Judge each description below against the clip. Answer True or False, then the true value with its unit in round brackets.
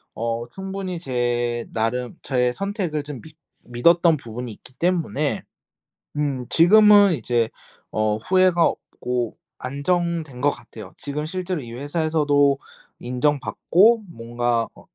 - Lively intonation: True (5.9 semitones)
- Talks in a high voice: False (145 Hz)